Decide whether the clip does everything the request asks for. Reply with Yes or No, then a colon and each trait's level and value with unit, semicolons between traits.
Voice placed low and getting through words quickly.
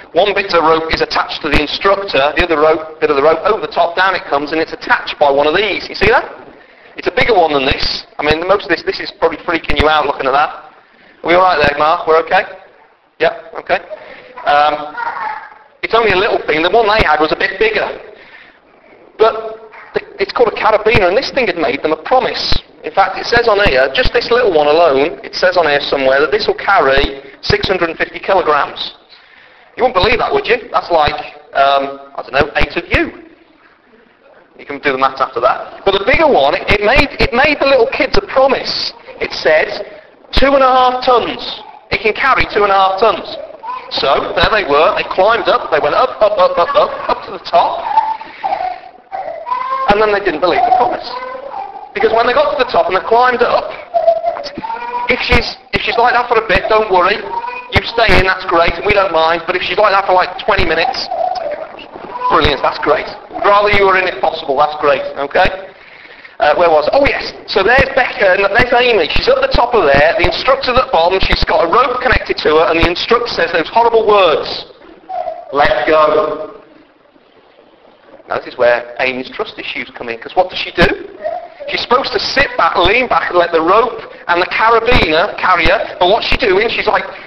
No: high, 205 Hz; fast, 215 wpm